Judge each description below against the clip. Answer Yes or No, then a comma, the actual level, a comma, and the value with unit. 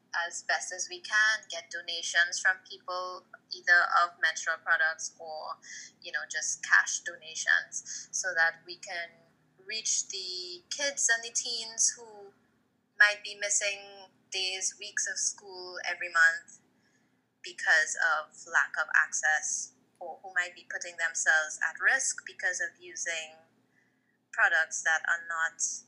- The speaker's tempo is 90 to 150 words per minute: Yes, slow, 135 wpm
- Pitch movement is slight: No, average, 4.3 semitones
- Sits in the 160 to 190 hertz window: Yes, medium, 185 Hz